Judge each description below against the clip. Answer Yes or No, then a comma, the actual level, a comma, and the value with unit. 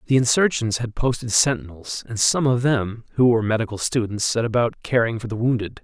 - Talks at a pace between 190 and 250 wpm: Yes, average, 195 wpm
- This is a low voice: Yes, low, 115 Hz